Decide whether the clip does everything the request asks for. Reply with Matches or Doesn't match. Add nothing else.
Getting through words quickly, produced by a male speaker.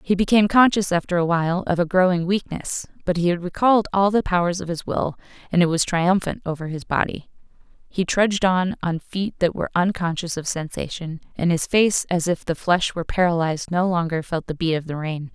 Doesn't match